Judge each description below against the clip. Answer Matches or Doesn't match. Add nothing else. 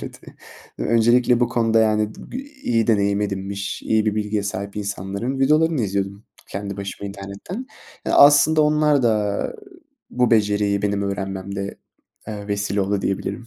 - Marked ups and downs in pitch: Doesn't match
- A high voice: Doesn't match